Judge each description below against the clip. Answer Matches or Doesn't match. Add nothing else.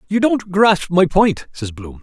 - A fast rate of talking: Matches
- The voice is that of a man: Matches